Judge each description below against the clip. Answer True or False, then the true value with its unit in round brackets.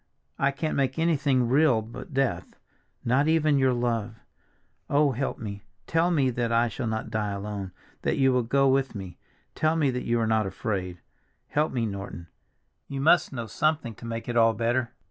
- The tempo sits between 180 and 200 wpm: True (185 wpm)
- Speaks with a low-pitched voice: True (120 Hz)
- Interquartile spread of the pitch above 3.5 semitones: True (3.9 semitones)